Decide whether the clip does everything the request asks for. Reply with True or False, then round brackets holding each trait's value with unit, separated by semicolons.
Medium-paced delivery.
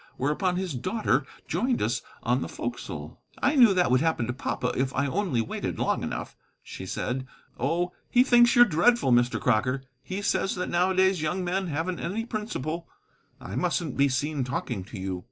True (180 wpm)